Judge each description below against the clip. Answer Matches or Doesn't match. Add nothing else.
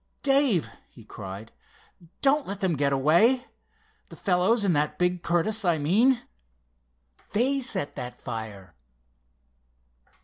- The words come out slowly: Matches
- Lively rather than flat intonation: Matches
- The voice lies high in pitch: Doesn't match